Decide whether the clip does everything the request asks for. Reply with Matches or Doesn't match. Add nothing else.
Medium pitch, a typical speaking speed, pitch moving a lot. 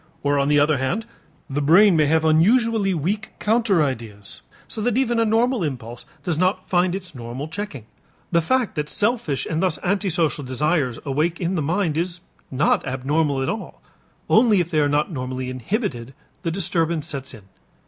Matches